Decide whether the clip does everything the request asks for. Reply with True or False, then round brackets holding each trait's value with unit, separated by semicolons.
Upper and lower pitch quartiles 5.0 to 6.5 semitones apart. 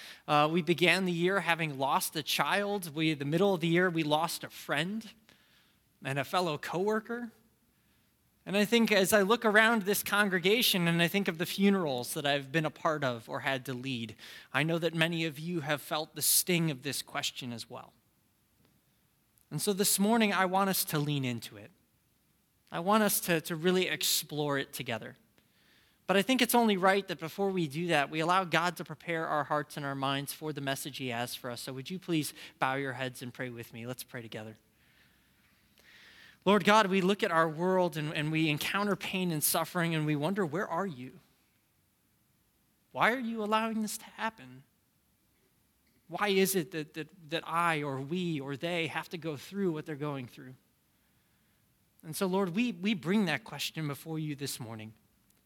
True (5.3 semitones)